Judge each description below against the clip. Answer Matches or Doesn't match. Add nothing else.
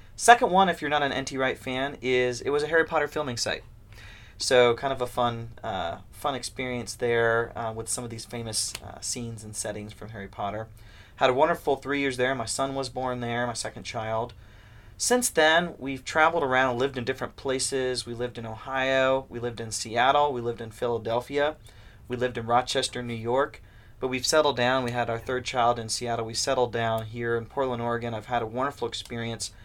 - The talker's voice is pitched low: Matches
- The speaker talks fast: Matches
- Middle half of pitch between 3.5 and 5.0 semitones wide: Doesn't match